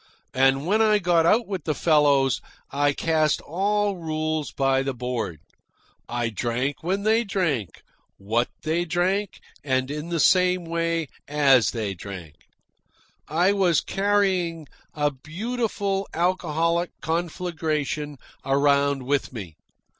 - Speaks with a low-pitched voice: No, medium, 155 Hz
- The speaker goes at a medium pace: No, slow, 120 wpm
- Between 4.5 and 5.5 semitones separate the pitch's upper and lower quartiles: Yes, average, 5.0 semitones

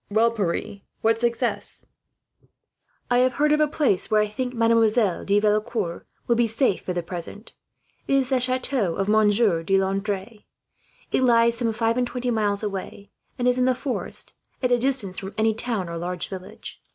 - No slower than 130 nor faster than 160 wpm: No, average, 185 wpm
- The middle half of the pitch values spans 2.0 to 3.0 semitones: No, average, 3.8 semitones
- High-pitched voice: Yes, high, 225 Hz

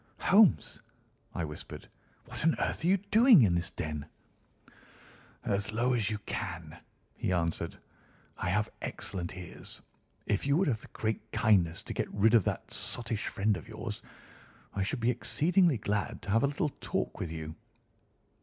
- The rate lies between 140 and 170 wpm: Yes, average, 165 wpm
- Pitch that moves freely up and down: Yes, wide, 7.3 semitones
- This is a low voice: Yes, low, 110 Hz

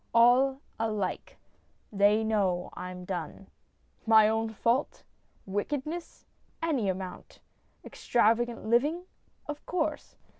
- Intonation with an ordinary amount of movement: Yes, average, 5.0 semitones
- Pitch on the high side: Yes, high, 225 Hz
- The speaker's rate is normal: No, slow, 90 wpm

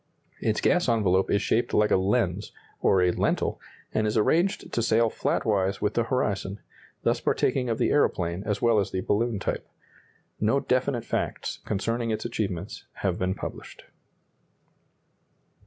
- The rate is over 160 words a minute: No, average, 155 wpm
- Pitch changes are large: No, average, 3.3 semitones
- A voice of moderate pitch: No, low, 105 Hz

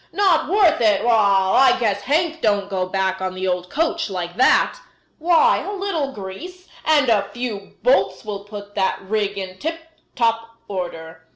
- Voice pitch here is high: Yes, high, 215 Hz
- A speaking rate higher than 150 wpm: Yes, average, 170 wpm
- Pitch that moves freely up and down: Yes, wide, 8.4 semitones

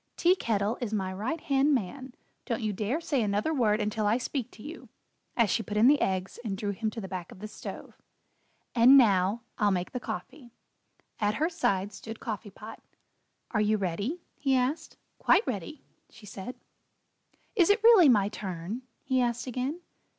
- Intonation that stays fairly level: No, average, 4.5 semitones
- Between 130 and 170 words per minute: No, average, 185 wpm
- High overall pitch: Yes, high, 225 Hz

